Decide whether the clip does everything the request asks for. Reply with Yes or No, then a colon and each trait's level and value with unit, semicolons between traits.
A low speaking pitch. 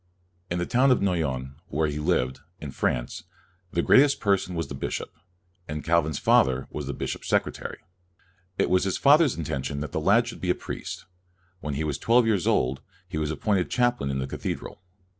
Yes: very low, 80 Hz